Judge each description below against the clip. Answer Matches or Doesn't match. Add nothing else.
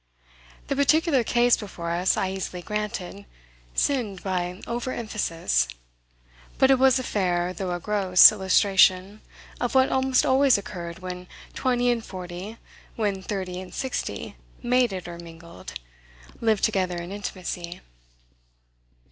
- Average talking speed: Doesn't match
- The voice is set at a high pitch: Matches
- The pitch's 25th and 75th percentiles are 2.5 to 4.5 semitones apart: Doesn't match